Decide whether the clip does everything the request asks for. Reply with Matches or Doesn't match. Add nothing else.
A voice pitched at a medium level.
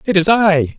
Matches